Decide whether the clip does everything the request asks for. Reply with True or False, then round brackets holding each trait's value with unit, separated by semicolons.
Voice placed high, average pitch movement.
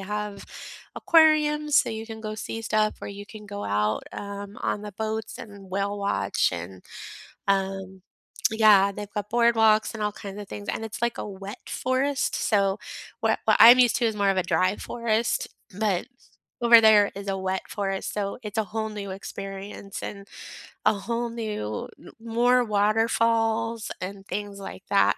False (210 Hz; 2.3 semitones)